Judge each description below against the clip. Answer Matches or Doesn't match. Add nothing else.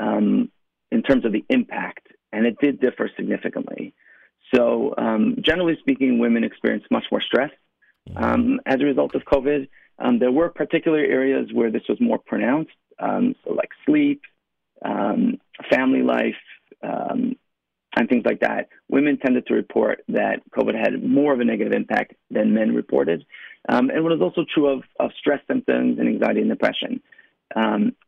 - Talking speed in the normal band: Matches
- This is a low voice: Doesn't match